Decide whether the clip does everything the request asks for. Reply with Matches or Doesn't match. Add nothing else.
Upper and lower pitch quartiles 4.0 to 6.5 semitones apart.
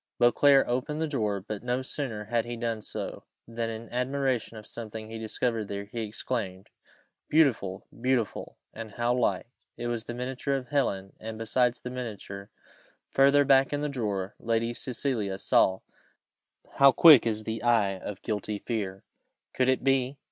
Doesn't match